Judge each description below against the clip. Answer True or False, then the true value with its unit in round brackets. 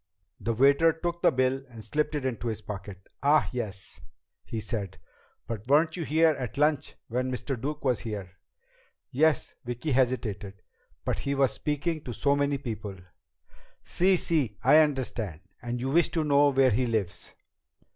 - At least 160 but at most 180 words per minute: True (170 wpm)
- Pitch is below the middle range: True (130 Hz)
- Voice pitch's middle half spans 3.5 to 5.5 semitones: True (4.9 semitones)